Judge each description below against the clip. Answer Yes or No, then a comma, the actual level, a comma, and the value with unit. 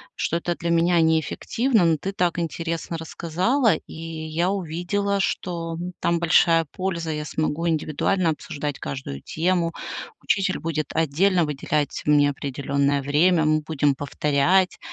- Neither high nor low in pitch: Yes, medium, 165 Hz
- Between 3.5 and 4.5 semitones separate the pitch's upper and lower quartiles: No, average, 2.7 semitones